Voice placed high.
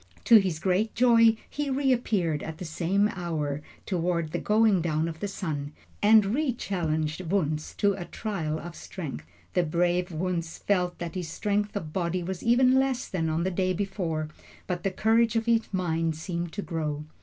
No: medium, 180 Hz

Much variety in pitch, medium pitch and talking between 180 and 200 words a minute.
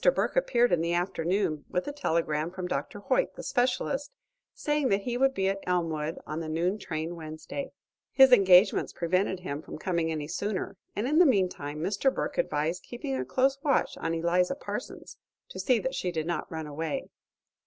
Yes: wide, 7.1 semitones; medium, 180 Hz; average, 185 wpm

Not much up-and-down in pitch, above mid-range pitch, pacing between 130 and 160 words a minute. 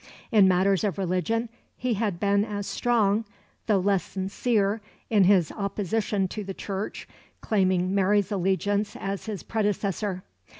Yes: narrow, 1.7 semitones; high, 200 Hz; slow, 135 wpm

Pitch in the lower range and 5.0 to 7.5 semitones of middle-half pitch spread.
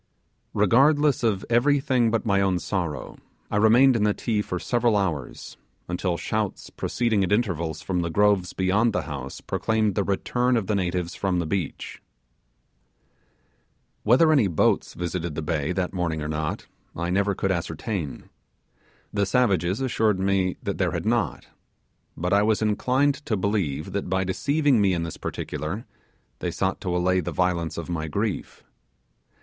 No: very low, 95 Hz; average, 4.2 semitones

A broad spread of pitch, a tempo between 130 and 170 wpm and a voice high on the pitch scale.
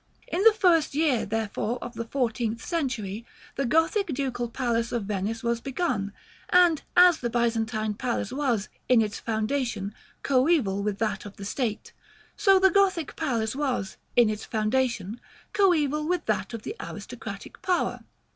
Yes: wide, 5.8 semitones; average, 155 wpm; high, 240 Hz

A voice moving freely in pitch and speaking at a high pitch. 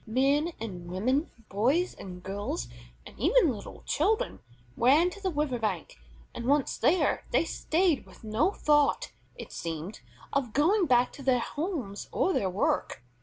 Yes: wide, 7.9 semitones; very high, 265 Hz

